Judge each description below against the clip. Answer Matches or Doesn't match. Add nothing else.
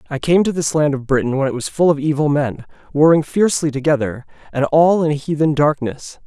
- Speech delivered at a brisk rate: Matches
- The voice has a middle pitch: Matches